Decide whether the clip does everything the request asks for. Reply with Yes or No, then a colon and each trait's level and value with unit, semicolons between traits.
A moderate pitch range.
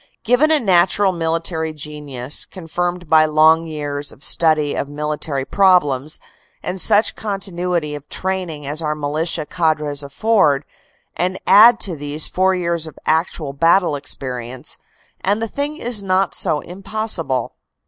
Yes: average, 4.2 semitones